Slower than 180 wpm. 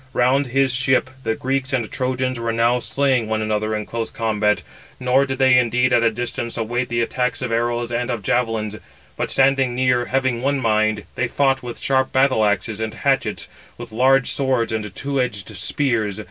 No: average, 190 wpm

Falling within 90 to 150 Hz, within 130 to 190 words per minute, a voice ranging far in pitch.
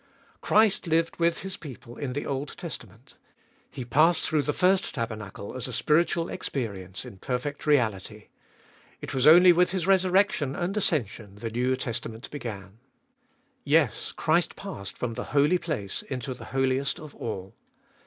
Yes: low, 135 Hz; average, 155 wpm; wide, 6.5 semitones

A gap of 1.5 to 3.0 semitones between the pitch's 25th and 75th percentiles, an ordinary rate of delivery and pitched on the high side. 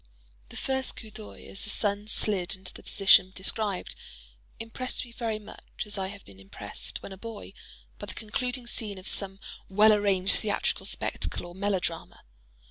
Yes: narrow, 2.5 semitones; average, 170 wpm; high, 205 Hz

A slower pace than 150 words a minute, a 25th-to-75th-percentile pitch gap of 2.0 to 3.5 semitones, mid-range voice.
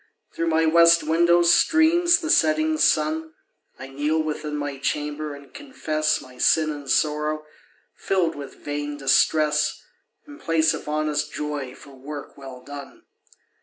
Yes: average, 140 wpm; narrow, 2.5 semitones; medium, 155 Hz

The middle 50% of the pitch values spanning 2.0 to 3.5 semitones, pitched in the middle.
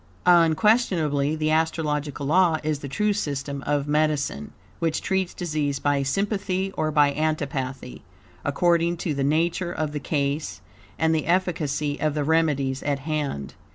Yes: average, 2.8 semitones; medium, 155 Hz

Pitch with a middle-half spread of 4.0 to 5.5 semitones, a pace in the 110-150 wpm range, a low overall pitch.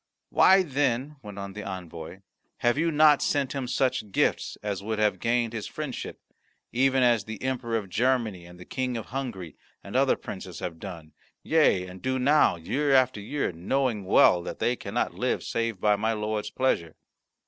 No: average, 5.1 semitones; average, 180 wpm; low, 115 Hz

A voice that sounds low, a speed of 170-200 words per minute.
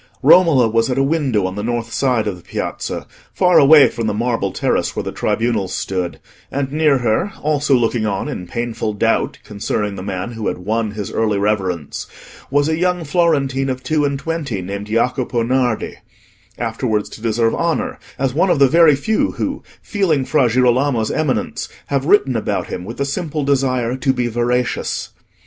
Yes: low, 125 Hz; average, 180 wpm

